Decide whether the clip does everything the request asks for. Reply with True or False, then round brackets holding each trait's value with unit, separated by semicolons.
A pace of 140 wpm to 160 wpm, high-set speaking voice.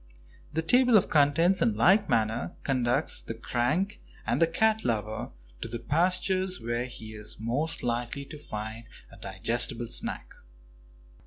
False (145 wpm; 125 Hz)